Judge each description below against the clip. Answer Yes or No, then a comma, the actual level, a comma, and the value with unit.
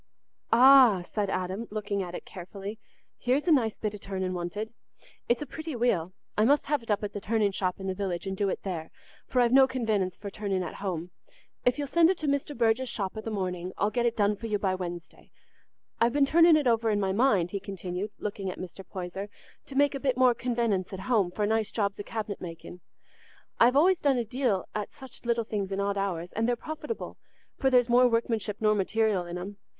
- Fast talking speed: Yes, fast, 225 wpm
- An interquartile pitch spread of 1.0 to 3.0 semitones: No, average, 4.3 semitones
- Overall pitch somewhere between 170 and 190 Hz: No, high, 210 Hz